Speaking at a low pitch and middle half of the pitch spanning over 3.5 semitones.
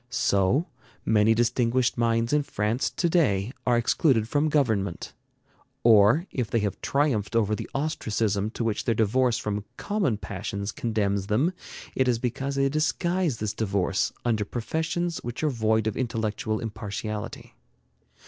Yes: low, 115 Hz; average, 4.3 semitones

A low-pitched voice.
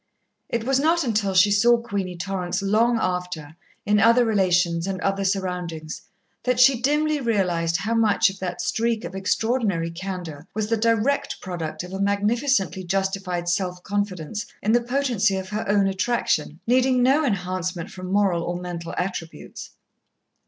No: high, 195 Hz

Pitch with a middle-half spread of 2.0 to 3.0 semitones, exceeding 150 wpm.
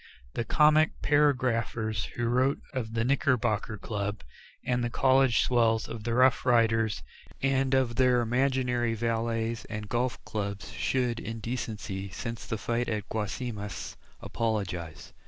No: narrow, 2.6 semitones; average, 145 wpm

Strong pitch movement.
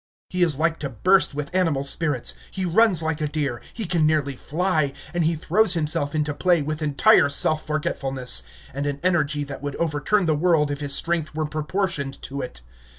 No: average, 3.1 semitones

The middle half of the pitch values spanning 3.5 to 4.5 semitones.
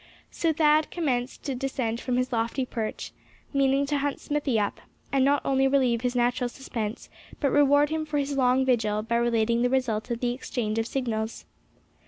No: average, 3.0 semitones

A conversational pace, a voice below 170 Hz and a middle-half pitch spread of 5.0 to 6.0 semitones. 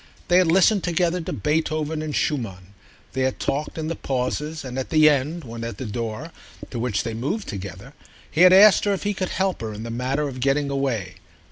No: fast, 220 wpm; medium, 140 Hz; wide, 5.6 semitones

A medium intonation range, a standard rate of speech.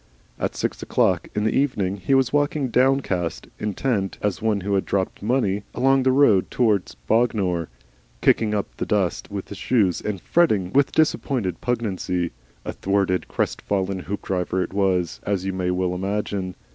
Yes: average, 4.4 semitones; average, 160 wpm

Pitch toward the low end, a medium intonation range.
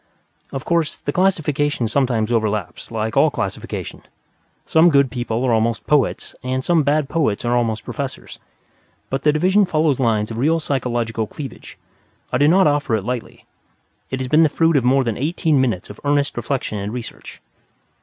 Yes: low, 130 Hz; average, 4.6 semitones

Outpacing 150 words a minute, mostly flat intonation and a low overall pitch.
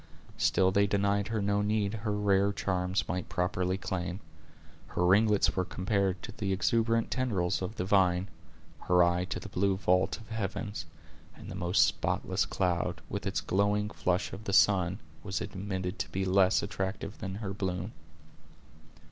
Yes: average, 165 wpm; narrow, 1.9 semitones; very low, 95 Hz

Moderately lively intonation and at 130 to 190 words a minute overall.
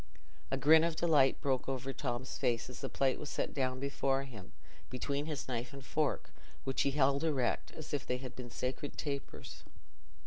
No: narrow, 2.0 semitones; average, 185 wpm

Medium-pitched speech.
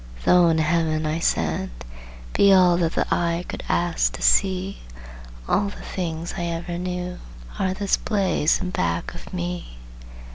Yes: medium, 170 Hz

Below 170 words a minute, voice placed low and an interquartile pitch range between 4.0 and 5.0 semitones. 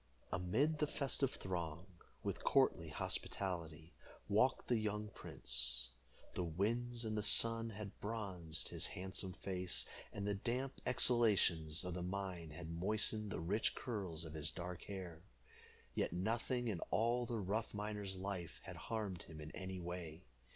Yes: average, 145 wpm; very low, 95 Hz; average, 4.3 semitones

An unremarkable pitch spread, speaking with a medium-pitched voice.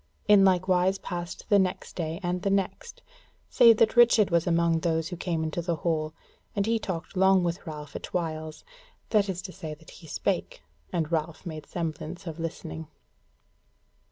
Yes: average, 3.0 semitones; medium, 175 Hz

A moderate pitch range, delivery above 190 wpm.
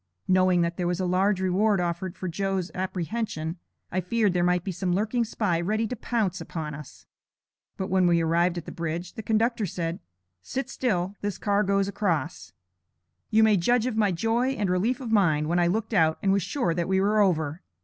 Yes: average, 3.6 semitones; fast, 205 wpm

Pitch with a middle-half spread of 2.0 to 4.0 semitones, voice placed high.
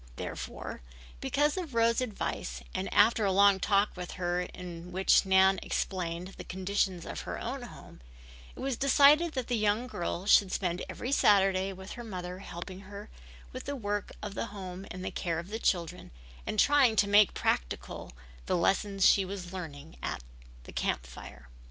Yes: average, 3.3 semitones; high, 195 Hz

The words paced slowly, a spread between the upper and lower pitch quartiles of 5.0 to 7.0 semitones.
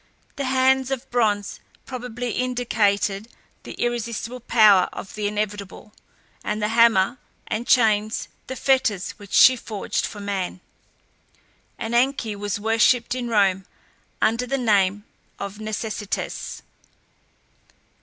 No: slow, 115 wpm; average, 3.2 semitones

